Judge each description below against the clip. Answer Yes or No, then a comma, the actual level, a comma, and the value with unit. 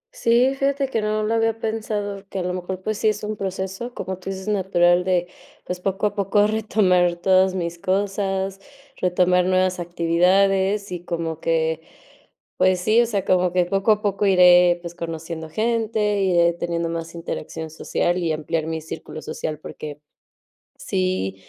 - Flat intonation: No, average, 3.2 semitones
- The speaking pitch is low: No, medium, 185 Hz